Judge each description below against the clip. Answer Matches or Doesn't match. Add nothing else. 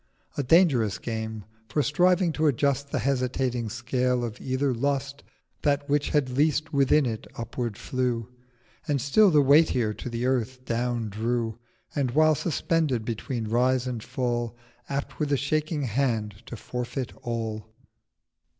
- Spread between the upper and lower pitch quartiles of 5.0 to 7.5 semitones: Doesn't match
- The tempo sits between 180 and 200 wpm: Doesn't match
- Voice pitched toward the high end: Doesn't match